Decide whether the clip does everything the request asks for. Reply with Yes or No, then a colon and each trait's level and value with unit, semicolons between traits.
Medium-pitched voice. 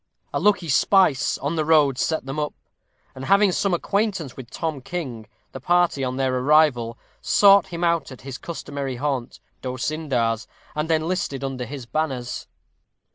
Yes: medium, 145 Hz